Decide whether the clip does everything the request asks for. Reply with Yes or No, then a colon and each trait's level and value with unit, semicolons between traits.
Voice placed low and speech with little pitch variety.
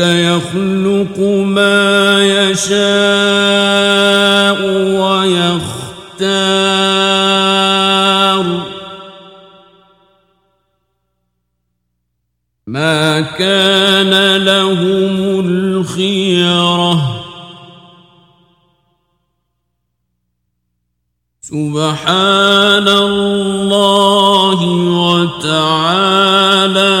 No: high, 190 Hz; narrow, 2.1 semitones